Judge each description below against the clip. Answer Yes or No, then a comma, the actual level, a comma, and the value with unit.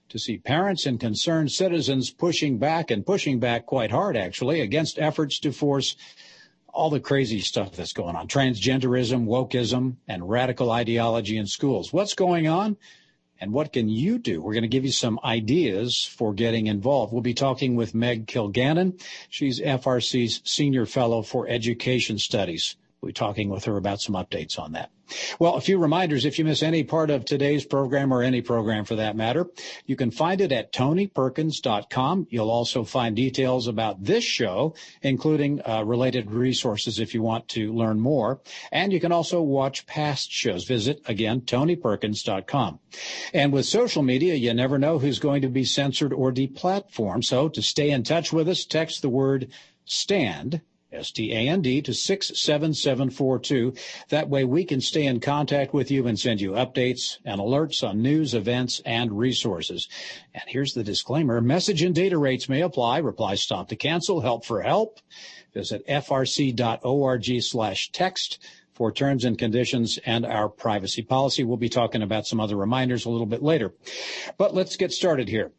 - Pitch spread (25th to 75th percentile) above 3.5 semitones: Yes, average, 4.1 semitones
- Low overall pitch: Yes, low, 130 Hz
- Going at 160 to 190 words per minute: Yes, average, 175 wpm